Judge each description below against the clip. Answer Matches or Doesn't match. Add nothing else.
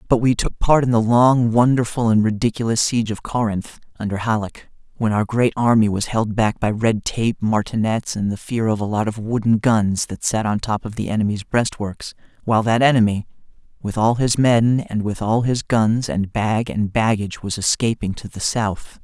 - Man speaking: Matches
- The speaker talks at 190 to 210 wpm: Matches